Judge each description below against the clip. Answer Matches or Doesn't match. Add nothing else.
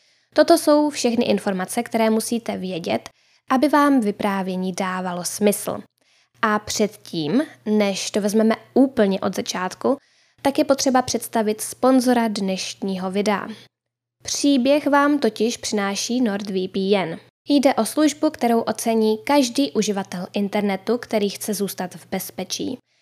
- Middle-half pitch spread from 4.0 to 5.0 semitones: Matches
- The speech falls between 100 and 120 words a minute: Matches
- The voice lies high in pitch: Matches